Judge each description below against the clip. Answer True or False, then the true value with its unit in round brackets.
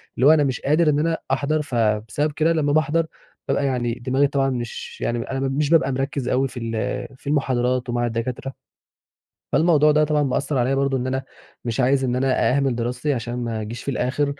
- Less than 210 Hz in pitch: True (135 Hz)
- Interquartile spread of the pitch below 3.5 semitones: True (3.0 semitones)